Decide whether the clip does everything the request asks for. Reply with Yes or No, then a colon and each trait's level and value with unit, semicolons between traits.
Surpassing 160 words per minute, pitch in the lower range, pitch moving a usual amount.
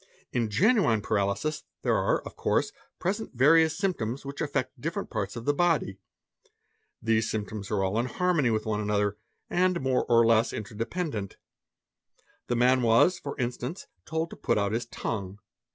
No: average, 185 wpm; low, 120 Hz; wide, 6.8 semitones